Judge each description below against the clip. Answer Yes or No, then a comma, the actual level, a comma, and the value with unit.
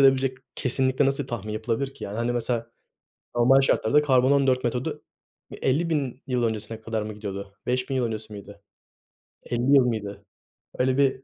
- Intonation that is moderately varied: Yes, average, 3.3 semitones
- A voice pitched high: No, low, 125 Hz